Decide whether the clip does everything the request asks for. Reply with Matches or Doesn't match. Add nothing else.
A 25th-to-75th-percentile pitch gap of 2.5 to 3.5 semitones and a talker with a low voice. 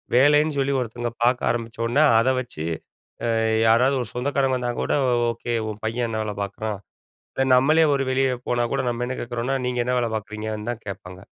Matches